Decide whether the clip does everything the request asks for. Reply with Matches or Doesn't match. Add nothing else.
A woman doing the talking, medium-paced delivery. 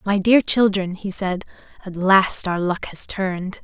Matches